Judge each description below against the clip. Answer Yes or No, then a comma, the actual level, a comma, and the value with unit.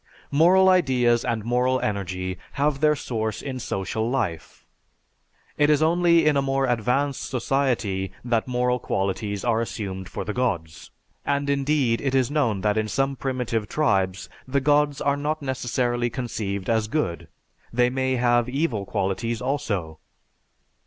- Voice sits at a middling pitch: No, low, 125 Hz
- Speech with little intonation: No, average, 4.7 semitones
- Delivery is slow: No, average, 150 wpm